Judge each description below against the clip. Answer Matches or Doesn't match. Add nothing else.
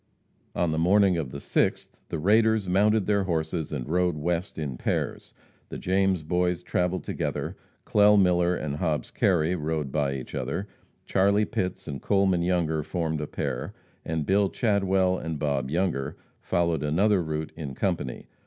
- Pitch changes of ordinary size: Matches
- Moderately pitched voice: Doesn't match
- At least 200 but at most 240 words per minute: Doesn't match